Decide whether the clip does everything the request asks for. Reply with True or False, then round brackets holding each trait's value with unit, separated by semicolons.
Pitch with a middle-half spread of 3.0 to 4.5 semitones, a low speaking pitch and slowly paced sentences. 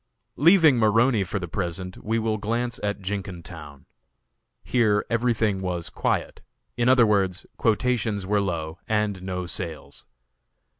True (3.8 semitones; 105 Hz; 130 wpm)